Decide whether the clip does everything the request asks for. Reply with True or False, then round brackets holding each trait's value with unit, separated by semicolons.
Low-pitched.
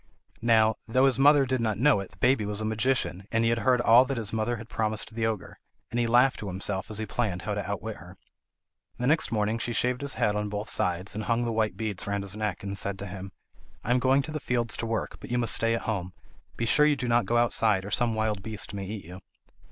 True (110 Hz)